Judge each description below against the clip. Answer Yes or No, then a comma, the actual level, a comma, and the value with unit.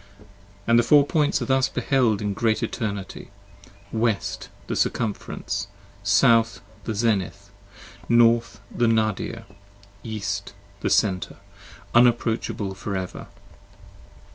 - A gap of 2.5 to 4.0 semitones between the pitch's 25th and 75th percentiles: Yes, average, 2.8 semitones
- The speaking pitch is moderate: No, low, 110 Hz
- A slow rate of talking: Yes, slow, 110 wpm